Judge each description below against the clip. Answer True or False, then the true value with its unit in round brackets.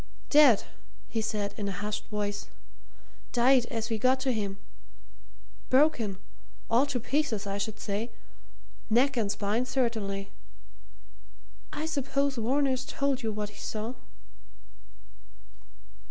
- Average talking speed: False (120 wpm)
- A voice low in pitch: False (230 Hz)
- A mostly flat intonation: False (4.2 semitones)